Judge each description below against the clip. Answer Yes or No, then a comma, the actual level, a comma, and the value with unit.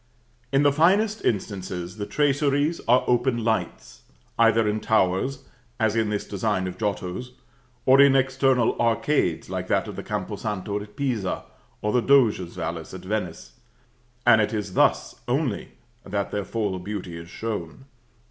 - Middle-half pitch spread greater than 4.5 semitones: Yes, average, 5.3 semitones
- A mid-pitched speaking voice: No, low, 110 Hz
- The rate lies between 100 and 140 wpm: No, average, 155 wpm